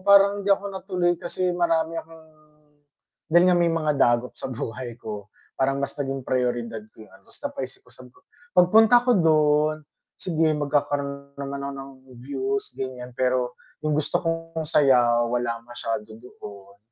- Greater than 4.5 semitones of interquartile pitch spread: Yes, average, 5.3 semitones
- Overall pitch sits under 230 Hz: Yes, medium, 140 Hz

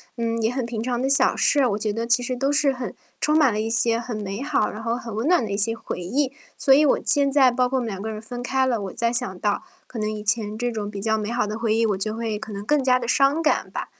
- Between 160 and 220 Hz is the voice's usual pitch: No, high, 230 Hz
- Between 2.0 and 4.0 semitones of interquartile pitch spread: Yes, average, 3.2 semitones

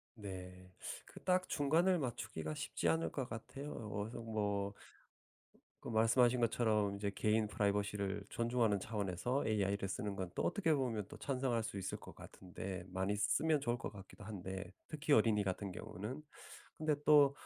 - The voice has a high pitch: No, low, 105 Hz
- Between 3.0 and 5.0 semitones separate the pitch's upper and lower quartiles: Yes, average, 4.0 semitones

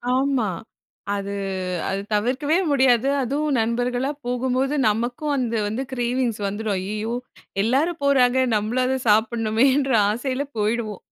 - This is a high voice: Yes, high, 245 Hz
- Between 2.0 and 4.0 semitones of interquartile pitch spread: Yes, average, 3.3 semitones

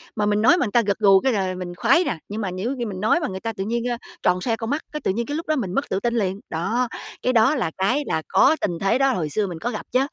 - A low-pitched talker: No, high, 220 Hz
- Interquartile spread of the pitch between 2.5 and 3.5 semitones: No, average, 4.8 semitones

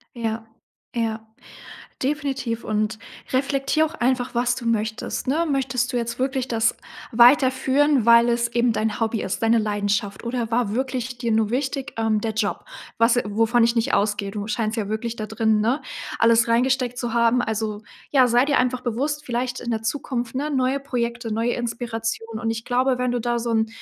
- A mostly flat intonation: Yes, narrow, 2.3 semitones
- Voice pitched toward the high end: Yes, high, 235 Hz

